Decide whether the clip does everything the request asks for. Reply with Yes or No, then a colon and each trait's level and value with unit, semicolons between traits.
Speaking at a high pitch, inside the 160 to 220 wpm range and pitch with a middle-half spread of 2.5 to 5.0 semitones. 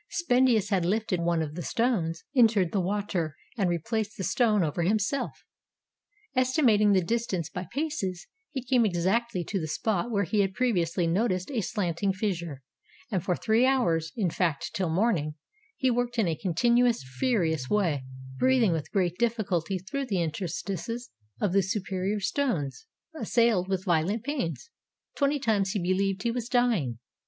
No: high, 200 Hz; average, 165 wpm; wide, 5.4 semitones